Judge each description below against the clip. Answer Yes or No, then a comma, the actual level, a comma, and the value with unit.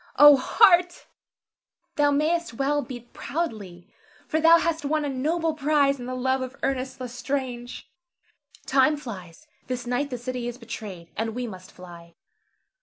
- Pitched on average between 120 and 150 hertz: No, very high, 260 Hz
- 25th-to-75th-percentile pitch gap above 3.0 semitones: Yes, average, 3.5 semitones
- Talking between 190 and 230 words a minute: No, average, 150 wpm